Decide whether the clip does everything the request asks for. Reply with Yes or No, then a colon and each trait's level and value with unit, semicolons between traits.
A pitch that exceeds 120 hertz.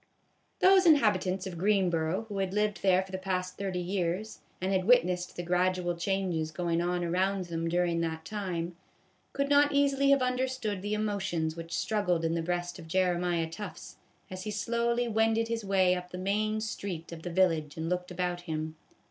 Yes: medium, 185 Hz